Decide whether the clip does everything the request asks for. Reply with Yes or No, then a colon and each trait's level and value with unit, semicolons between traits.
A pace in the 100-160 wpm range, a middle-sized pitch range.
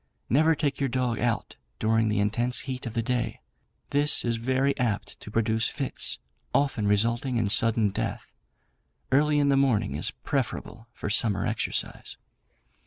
Yes: average, 155 wpm; average, 3.4 semitones